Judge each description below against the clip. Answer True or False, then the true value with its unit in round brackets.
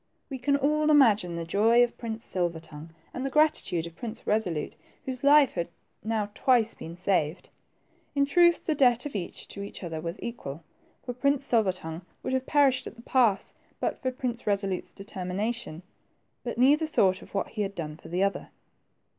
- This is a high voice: True (220 Hz)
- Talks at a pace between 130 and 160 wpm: False (190 wpm)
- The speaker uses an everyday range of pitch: False (6.3 semitones)